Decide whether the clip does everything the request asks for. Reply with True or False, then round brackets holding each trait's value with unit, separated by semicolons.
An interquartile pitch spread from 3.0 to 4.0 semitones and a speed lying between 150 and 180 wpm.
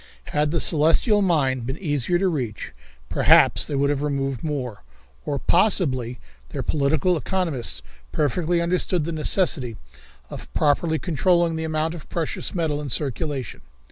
False (3.7 semitones; 140 wpm)